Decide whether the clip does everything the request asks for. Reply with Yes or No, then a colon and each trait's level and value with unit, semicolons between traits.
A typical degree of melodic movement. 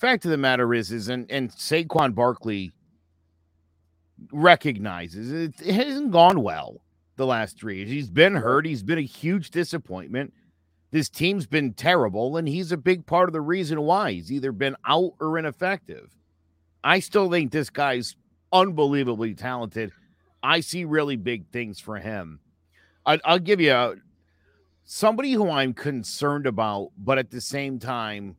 No: wide, 8.4 semitones